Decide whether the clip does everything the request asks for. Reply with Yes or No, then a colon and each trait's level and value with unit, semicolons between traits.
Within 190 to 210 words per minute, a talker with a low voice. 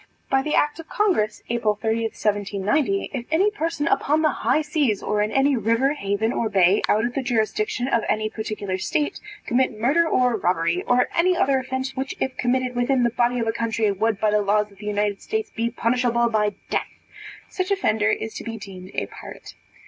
No: average, 200 wpm; high, 235 Hz